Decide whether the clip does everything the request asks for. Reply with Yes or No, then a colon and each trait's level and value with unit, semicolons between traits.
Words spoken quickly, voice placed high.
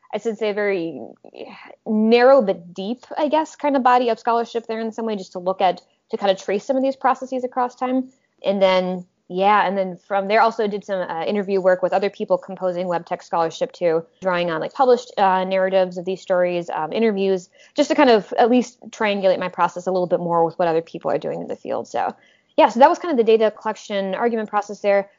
Yes: fast, 240 wpm; high, 200 Hz